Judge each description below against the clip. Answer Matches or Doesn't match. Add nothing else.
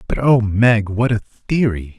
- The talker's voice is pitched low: Matches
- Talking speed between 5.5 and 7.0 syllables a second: Doesn't match